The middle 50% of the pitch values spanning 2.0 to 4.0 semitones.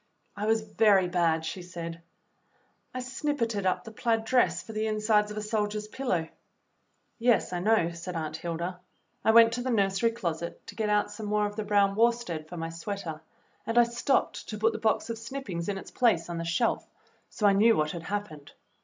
No: average, 4.7 semitones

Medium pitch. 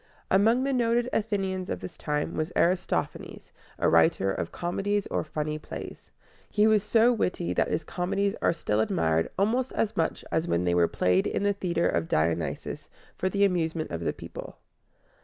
Yes: medium, 180 Hz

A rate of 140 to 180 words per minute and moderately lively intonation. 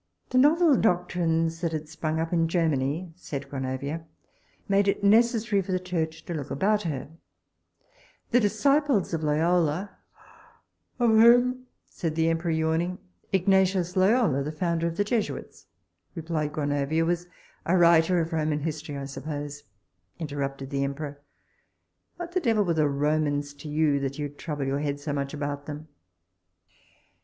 Yes: average, 150 wpm; average, 4.2 semitones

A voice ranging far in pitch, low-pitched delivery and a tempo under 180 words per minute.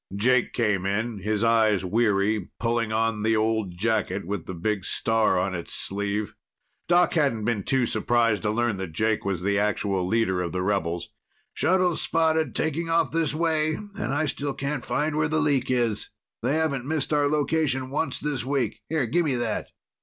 No: wide, 6.3 semitones; low, 115 Hz; average, 185 wpm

